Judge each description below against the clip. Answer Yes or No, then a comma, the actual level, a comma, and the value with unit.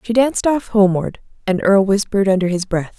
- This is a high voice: Yes, high, 205 Hz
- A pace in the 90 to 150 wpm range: No, average, 200 wpm